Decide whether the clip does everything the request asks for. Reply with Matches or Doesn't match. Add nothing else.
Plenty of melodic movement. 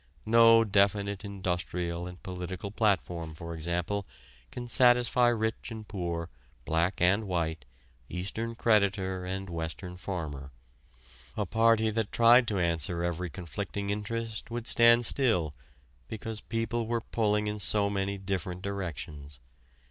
Doesn't match